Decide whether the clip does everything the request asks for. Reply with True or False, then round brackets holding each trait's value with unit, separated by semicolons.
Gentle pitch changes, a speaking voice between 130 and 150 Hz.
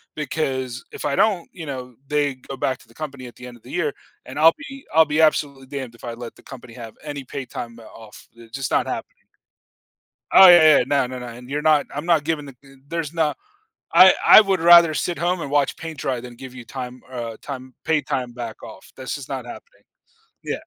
False (3.9 semitones; 140 Hz)